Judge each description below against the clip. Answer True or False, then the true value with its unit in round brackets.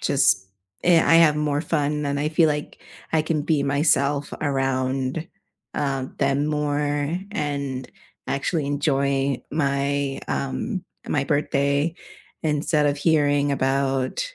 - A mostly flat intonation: True (1.6 semitones)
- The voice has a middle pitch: True (145 Hz)